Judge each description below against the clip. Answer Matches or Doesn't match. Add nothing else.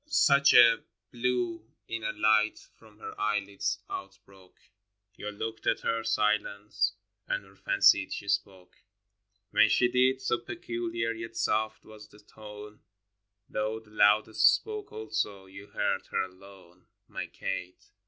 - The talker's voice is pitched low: Matches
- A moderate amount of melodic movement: Doesn't match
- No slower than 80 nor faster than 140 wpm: Matches